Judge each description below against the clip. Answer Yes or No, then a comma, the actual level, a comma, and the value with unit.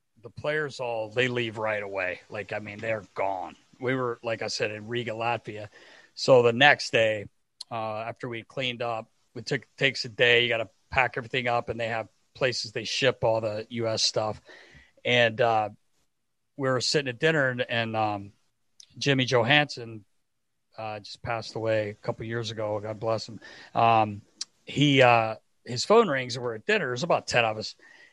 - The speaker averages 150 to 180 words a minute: No, average, 190 wpm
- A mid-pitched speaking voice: No, low, 115 Hz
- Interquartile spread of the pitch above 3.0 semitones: No, narrow, 2.5 semitones